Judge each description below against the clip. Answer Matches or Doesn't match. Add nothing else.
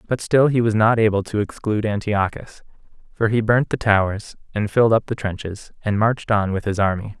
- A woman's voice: Doesn't match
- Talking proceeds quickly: Matches